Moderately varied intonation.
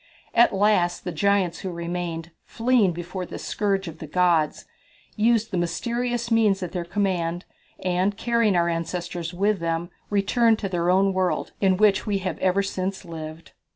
Yes: average, 3.1 semitones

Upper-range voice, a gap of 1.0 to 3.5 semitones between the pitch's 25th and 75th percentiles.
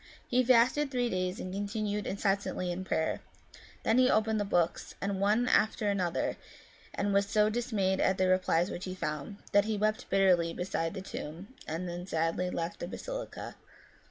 Yes: high, 195 Hz; average, 2.9 semitones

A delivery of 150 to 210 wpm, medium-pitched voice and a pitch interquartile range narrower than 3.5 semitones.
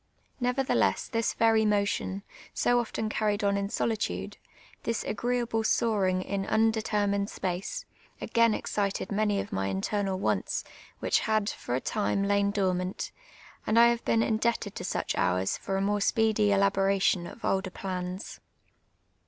No: average, 155 wpm; high, 205 Hz; narrow, 2.4 semitones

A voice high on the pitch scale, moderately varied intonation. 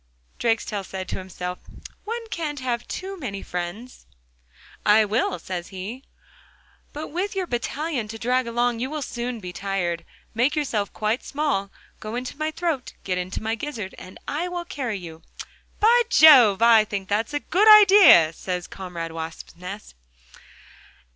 No: high, 230 Hz; wide, 7.6 semitones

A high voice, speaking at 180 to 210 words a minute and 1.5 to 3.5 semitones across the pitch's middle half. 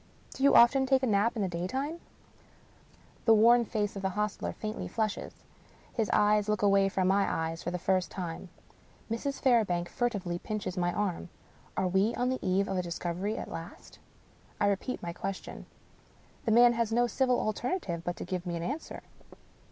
No: high, 205 Hz; average, 190 wpm; average, 4.5 semitones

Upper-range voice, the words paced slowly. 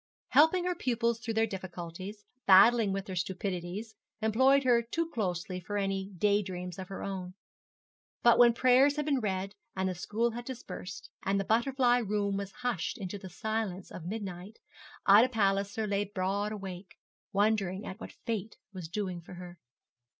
No: high, 200 Hz; average, 165 wpm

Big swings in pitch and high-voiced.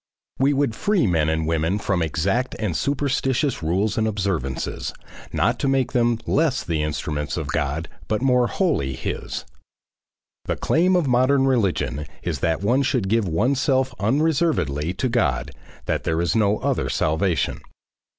No: wide, 8.7 semitones; low, 105 Hz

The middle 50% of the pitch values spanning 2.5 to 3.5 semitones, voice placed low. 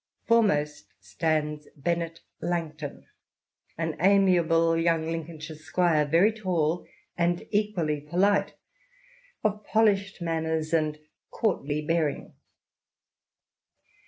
No: average, 2.9 semitones; medium, 165 Hz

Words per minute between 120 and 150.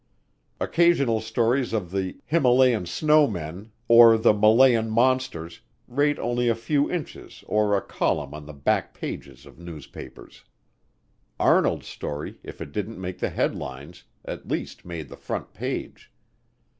Yes: slow, 135 wpm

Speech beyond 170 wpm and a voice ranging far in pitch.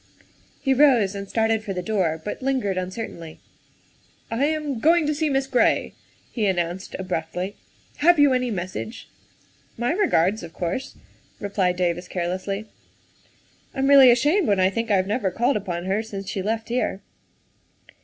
Yes: average, 180 wpm; wide, 5.9 semitones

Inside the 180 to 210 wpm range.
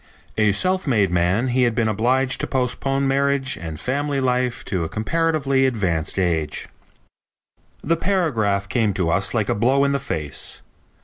No: average, 165 wpm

